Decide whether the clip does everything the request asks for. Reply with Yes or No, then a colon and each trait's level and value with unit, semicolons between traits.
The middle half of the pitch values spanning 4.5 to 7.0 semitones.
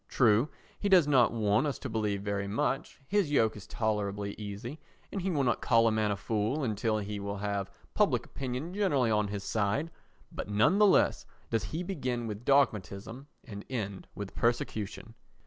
Yes: average, 5.1 semitones